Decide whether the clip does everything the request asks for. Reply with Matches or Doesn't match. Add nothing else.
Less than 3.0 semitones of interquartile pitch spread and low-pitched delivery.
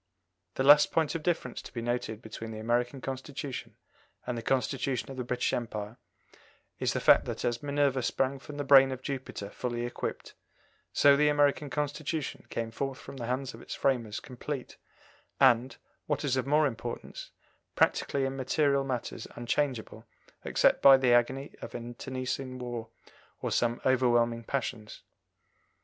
Matches